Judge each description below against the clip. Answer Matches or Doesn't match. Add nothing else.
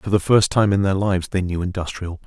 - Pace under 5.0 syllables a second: Doesn't match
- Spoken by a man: Matches